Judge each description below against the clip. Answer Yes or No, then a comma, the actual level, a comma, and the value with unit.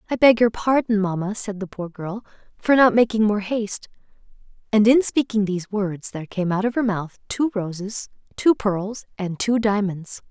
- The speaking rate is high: No, average, 185 wpm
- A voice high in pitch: Yes, high, 210 Hz